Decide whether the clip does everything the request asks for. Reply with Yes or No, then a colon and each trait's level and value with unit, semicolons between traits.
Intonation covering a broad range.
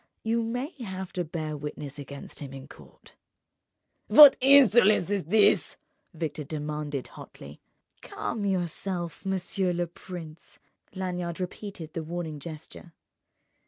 No: average, 4.3 semitones